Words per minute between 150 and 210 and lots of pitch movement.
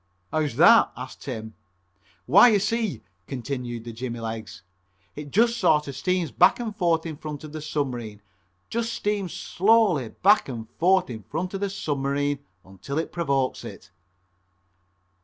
Yes: average, 155 wpm; wide, 7.0 semitones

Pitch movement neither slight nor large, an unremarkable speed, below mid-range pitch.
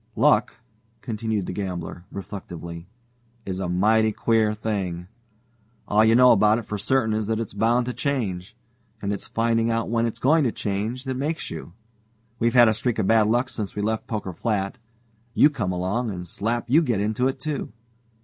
Yes: average, 3.2 semitones; average, 190 wpm; low, 110 Hz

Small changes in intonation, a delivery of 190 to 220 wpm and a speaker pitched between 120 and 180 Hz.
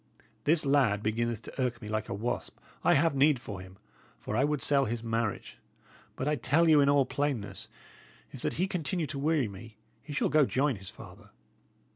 No: average, 4.8 semitones; fast, 205 wpm; low, 135 Hz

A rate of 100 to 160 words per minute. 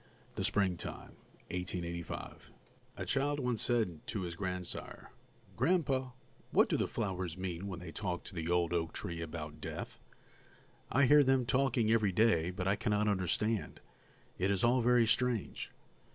Yes: average, 155 wpm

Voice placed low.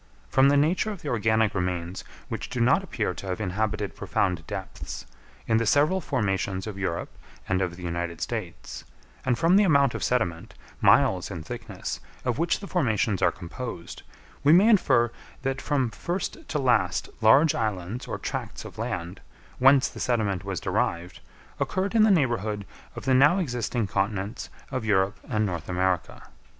Yes: low, 110 Hz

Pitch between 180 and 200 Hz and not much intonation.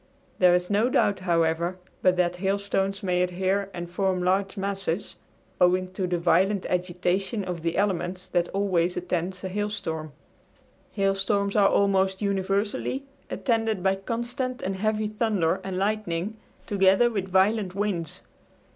Yes: high, 190 Hz; narrow, 2.0 semitones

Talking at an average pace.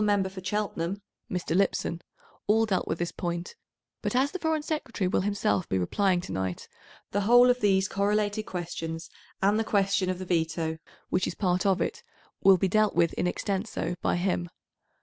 Yes: average, 185 wpm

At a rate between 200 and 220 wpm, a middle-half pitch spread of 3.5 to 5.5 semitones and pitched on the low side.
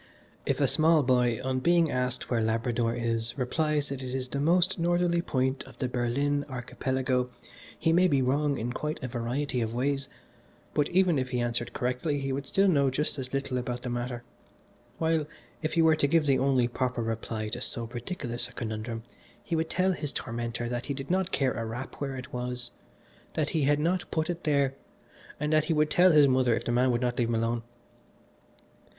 Yes: fast, 205 wpm; average, 3.8 semitones; low, 130 Hz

